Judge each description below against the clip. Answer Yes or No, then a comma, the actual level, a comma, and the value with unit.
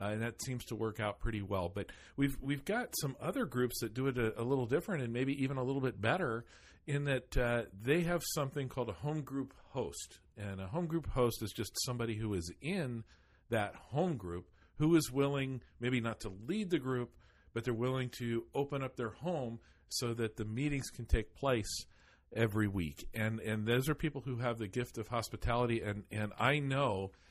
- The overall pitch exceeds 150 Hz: No, low, 120 Hz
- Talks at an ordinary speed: No, fast, 210 wpm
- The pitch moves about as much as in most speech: Yes, average, 3.9 semitones